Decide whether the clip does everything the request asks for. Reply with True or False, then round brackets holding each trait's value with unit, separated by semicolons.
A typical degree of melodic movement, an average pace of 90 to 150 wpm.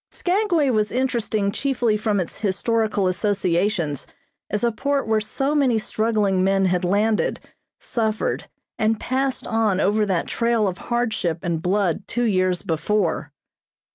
True (3.8 semitones; 140 wpm)